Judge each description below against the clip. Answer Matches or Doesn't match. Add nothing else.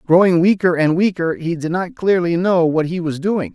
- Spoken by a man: Matches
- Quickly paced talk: Matches